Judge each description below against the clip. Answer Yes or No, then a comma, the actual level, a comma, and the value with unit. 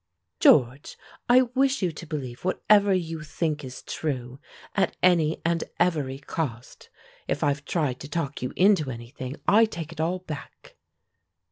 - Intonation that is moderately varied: Yes, average, 5.0 semitones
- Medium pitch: Yes, medium, 155 Hz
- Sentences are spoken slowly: No, average, 150 wpm